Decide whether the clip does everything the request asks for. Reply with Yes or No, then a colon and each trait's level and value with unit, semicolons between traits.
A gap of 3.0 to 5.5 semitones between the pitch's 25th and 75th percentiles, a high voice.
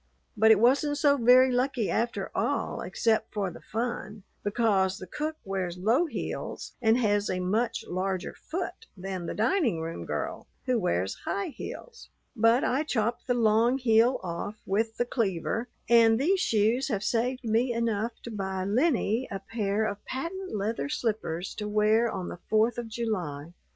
Yes: average, 3.7 semitones; high, 225 Hz